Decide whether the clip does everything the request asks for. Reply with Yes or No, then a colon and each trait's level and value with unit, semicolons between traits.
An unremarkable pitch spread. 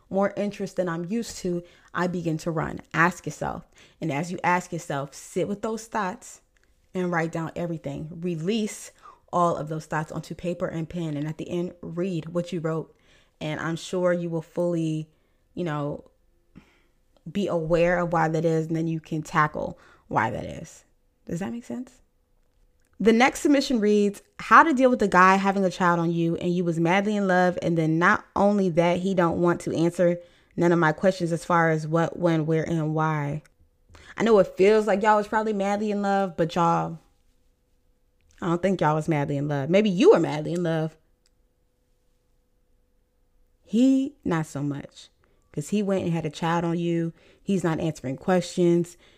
Yes: average, 3.0 semitones